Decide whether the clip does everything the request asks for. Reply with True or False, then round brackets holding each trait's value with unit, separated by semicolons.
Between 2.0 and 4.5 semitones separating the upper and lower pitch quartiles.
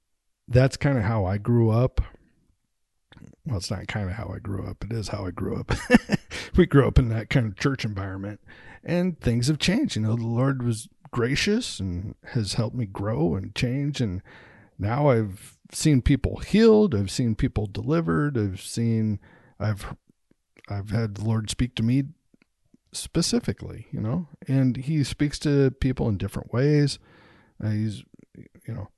False (5.1 semitones)